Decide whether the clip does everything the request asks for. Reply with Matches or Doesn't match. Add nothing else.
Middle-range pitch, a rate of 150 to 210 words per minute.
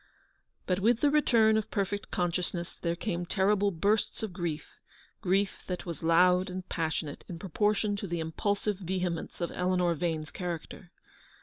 Matches